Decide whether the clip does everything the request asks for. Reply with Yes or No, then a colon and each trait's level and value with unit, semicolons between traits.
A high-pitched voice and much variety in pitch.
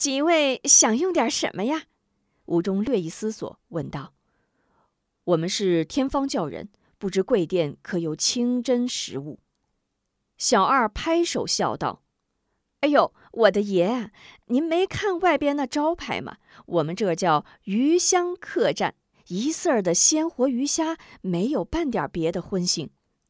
Yes: very high, 250 Hz; wide, 8.6 semitones